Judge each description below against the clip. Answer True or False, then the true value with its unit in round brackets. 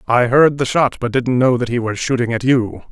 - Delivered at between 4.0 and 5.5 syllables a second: True (5.2 syllables/s)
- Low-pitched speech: True (125 Hz)